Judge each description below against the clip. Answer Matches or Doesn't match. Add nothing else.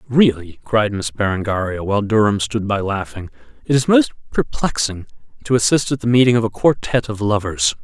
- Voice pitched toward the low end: Matches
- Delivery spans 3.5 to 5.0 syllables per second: Doesn't match